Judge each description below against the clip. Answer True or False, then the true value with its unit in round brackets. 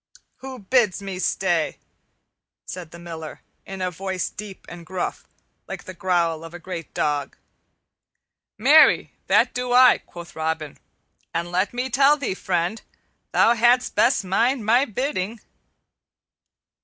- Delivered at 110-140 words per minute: True (135 wpm)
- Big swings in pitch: True (6.0 semitones)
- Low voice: False (190 Hz)